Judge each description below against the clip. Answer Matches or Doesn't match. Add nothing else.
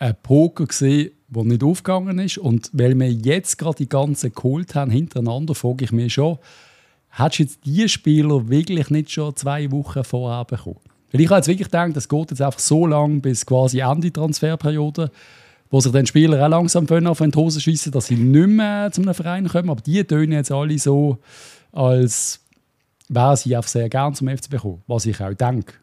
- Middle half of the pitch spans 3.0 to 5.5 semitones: Matches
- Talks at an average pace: Doesn't match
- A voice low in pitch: Doesn't match